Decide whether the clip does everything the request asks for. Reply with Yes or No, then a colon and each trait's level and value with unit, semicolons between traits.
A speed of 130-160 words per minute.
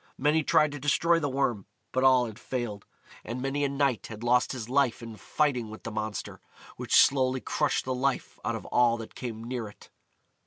No: average, 200 wpm